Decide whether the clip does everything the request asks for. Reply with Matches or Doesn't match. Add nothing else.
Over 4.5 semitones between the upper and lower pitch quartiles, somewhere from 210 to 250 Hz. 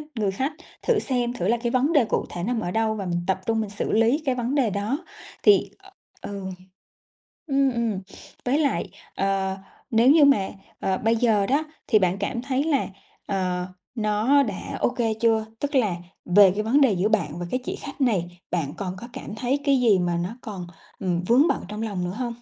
Matches